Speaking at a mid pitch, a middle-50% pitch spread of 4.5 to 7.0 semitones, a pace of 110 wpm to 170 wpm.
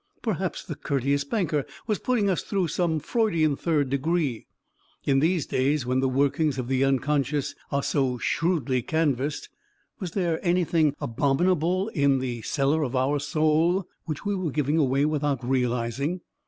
No: medium, 145 Hz; average, 3.8 semitones; average, 155 wpm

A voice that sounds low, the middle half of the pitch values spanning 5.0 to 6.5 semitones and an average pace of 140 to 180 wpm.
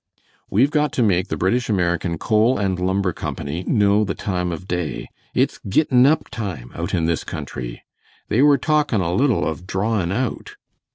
Yes: low, 100 Hz; wide, 5.6 semitones; average, 175 wpm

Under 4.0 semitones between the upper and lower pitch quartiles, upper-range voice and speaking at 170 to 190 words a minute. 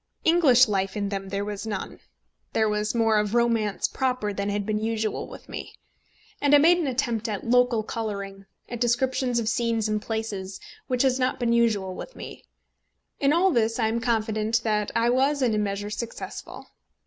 Yes: average, 2.9 semitones; high, 225 Hz; average, 185 wpm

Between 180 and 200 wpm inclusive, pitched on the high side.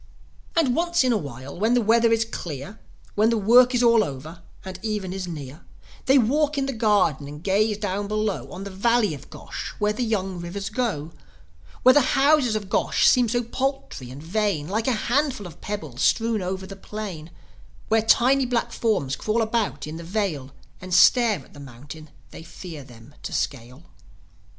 Yes: average, 190 wpm; high, 205 Hz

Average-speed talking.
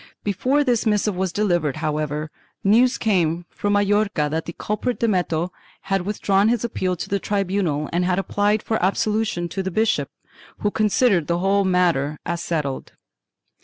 Yes: average, 160 wpm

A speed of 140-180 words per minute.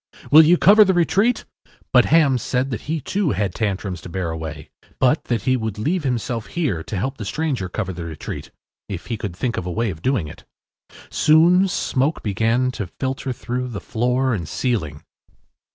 No: average, 190 wpm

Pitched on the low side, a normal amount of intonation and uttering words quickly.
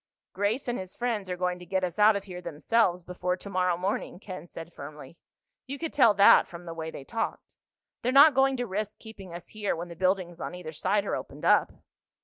No: medium, 185 Hz; average, 3.5 semitones; fast, 220 wpm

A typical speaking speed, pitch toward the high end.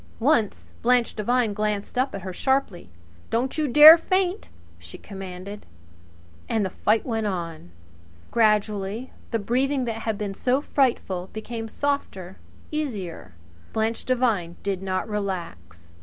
No: slow, 130 wpm; high, 215 Hz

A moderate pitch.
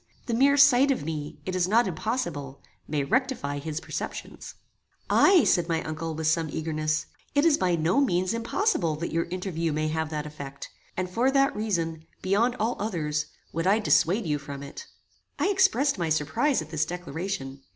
Yes: medium, 170 Hz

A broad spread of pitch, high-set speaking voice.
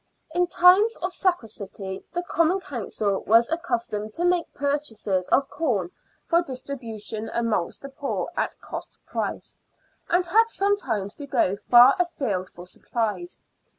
Yes: wide, 8.6 semitones; very high, 270 Hz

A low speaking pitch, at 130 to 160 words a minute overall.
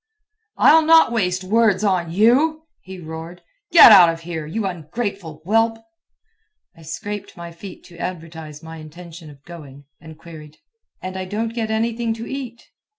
No: medium, 185 Hz; average, 155 wpm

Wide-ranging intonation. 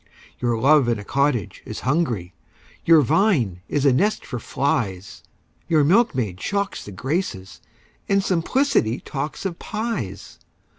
Yes: wide, 8.5 semitones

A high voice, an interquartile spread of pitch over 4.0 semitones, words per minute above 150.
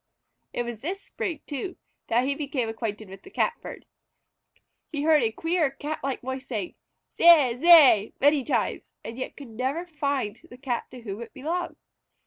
Yes: very high, 270 Hz; average, 4.8 semitones; average, 170 wpm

